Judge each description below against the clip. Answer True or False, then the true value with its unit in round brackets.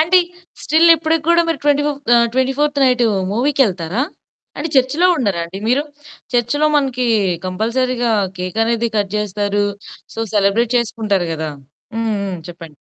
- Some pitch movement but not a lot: False (5.8 semitones)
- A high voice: True (240 Hz)